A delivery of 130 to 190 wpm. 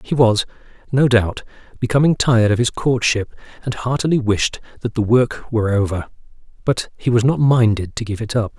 Yes: average, 180 wpm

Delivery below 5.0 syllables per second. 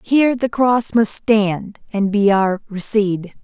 Yes: 3.5 syllables/s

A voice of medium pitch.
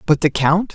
Yes: medium, 165 Hz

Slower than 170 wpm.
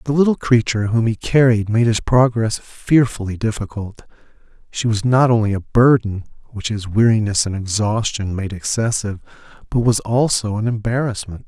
Yes: average, 150 wpm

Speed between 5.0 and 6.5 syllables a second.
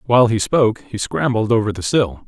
Yes: 5.8 syllables/s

